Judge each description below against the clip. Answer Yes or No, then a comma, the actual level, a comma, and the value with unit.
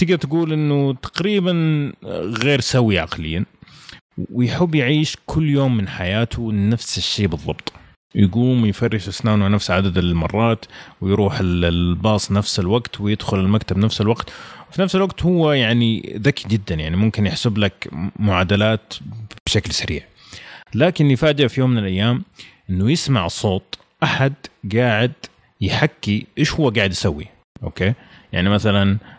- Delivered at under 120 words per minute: No, average, 130 wpm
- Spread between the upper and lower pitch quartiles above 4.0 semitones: Yes, wide, 5.4 semitones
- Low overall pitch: Yes, low, 110 Hz